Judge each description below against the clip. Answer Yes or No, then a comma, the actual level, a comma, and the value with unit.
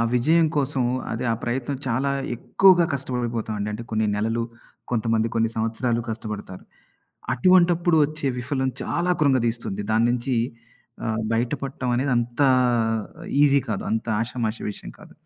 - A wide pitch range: No, average, 3.6 semitones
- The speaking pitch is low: Yes, low, 120 Hz